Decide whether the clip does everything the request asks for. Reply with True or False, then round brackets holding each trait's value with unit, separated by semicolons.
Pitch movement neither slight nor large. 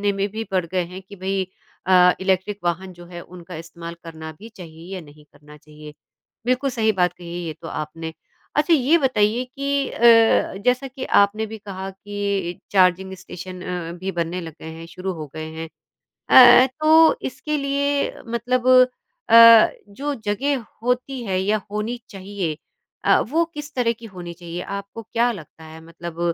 False (5.9 semitones)